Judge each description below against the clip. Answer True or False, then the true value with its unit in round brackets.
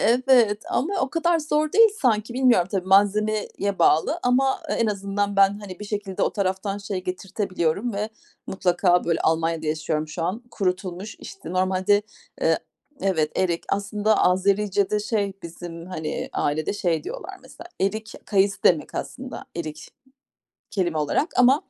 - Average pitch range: True (3.3 semitones)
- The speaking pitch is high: True (200 Hz)